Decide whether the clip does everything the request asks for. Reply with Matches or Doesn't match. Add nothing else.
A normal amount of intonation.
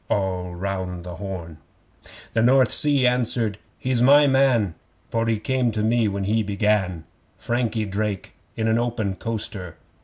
Matches